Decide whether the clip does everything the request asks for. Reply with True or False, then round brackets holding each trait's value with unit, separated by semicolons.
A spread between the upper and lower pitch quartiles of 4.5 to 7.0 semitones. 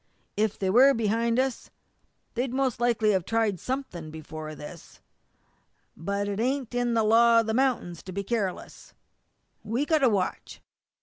False (3.9 semitones)